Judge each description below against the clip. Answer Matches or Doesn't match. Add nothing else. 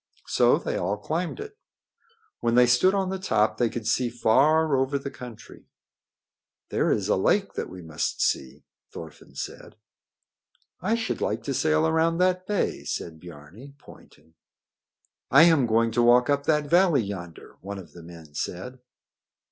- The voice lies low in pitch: Matches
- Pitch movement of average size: Doesn't match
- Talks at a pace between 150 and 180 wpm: Matches